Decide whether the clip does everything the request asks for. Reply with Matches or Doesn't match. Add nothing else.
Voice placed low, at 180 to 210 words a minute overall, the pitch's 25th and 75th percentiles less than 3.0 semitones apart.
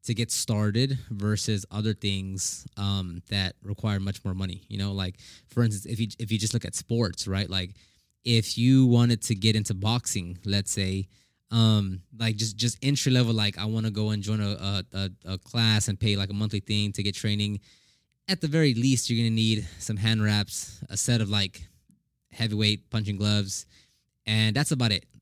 Matches